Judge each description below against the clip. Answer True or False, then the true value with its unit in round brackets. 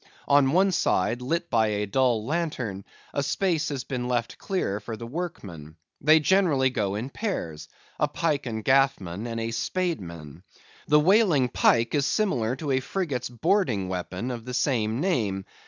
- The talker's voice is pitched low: True (125 Hz)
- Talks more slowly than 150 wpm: False (165 wpm)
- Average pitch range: False (6.2 semitones)